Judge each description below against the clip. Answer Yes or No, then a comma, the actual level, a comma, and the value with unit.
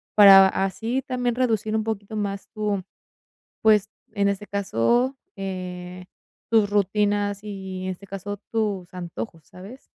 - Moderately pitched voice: No, high, 200 Hz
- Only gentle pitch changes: Yes, narrow, 2.2 semitones